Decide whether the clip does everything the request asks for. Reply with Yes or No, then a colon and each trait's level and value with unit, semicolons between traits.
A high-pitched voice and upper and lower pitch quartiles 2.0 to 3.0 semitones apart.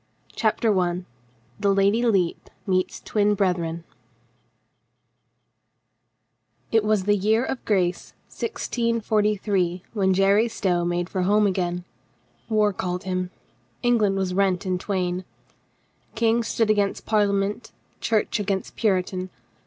Yes: high, 195 Hz; average, 2.7 semitones